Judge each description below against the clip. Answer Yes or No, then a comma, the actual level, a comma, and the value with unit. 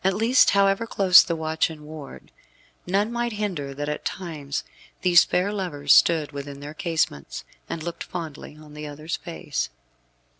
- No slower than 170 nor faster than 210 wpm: No, average, 160 wpm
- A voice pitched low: No, medium, 160 Hz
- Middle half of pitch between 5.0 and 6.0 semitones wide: No, average, 4.4 semitones